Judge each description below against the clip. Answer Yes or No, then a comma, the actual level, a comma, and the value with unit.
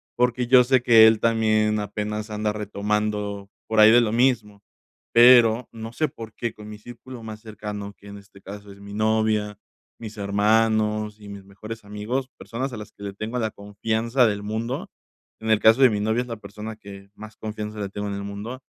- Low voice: Yes, low, 110 Hz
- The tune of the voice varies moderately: No, narrow, 1.7 semitones